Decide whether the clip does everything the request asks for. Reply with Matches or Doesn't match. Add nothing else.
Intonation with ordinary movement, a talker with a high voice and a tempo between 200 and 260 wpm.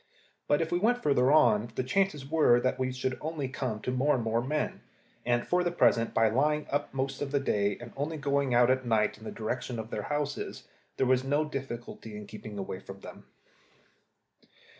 Doesn't match